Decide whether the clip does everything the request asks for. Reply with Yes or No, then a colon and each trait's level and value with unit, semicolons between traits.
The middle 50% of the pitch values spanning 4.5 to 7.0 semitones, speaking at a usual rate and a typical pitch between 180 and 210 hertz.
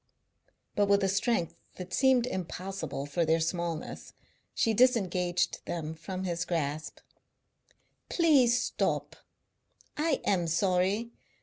No: average, 5.1 semitones; slow, 110 wpm; medium, 185 Hz